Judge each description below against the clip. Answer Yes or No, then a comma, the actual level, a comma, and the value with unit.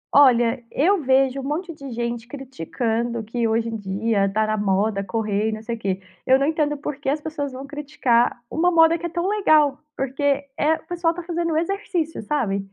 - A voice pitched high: Yes, very high, 270 Hz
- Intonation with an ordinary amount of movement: No, wide, 5.7 semitones